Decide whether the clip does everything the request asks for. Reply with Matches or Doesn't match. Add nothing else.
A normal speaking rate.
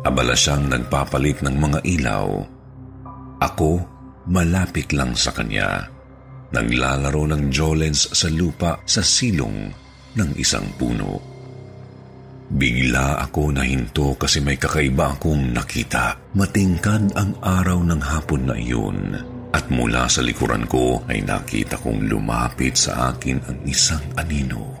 Matches